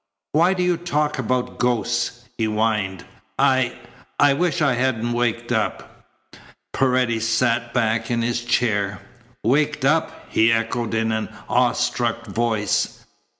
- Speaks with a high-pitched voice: No, low, 120 Hz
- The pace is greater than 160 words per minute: No, slow, 135 wpm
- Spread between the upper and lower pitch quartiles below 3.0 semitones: Yes, narrow, 2.5 semitones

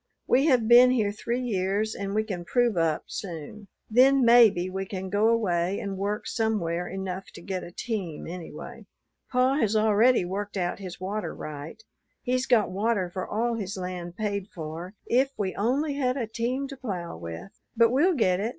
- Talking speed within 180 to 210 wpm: Yes, average, 185 wpm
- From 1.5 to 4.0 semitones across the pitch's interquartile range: No, average, 4.5 semitones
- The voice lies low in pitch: No, high, 205 Hz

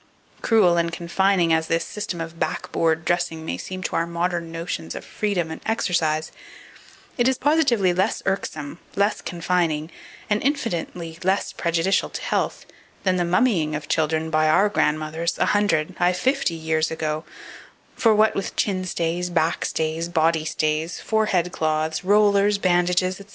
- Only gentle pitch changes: No, average, 3.4 semitones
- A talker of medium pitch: Yes, medium, 170 Hz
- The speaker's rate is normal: Yes, average, 155 wpm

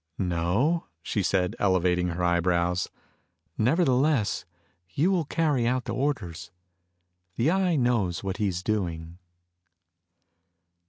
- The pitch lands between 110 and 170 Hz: No, low, 100 Hz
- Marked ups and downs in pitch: Yes, wide, 7.3 semitones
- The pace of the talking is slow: Yes, slow, 105 wpm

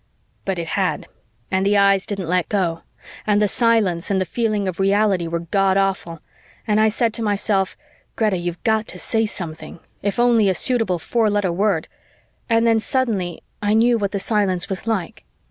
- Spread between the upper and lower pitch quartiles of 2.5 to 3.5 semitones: Yes, average, 2.9 semitones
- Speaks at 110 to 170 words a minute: No, average, 180 wpm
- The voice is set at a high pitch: Yes, high, 200 Hz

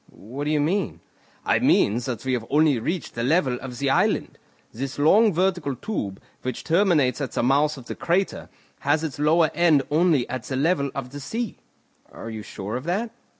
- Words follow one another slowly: No, average, 195 wpm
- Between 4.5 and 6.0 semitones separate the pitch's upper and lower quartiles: Yes, average, 5.1 semitones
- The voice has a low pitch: No, medium, 145 Hz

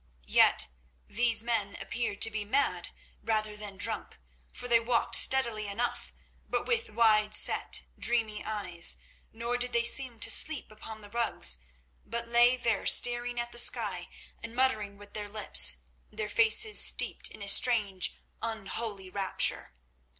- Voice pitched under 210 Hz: No, high, 225 Hz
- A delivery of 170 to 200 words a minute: No, average, 150 wpm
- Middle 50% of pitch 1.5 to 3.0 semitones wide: Yes, narrow, 2.6 semitones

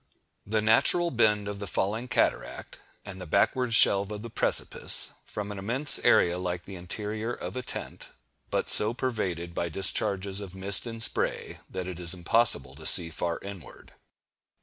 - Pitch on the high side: No, low, 100 Hz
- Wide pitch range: No, average, 3.5 semitones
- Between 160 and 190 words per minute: Yes, average, 170 wpm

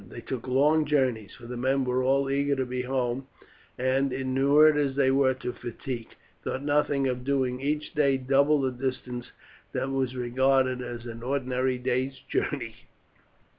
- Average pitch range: No, narrow, 1.6 semitones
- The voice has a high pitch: No, low, 130 Hz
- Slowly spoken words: No, average, 165 wpm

